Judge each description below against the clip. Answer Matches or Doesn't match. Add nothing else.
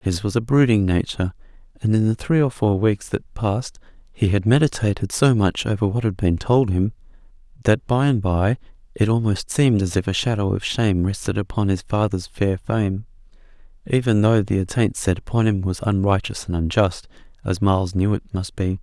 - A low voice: Matches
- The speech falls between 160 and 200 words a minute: Matches